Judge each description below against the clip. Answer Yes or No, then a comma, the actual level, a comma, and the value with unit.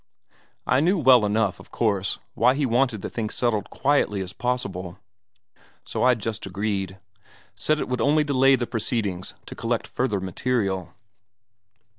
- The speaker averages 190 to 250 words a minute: No, average, 150 wpm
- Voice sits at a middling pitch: No, low, 115 Hz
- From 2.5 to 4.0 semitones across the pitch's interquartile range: No, average, 4.5 semitones